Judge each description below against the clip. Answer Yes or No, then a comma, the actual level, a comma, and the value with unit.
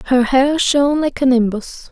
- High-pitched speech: Yes, very high, 265 Hz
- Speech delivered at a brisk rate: No, average, 190 wpm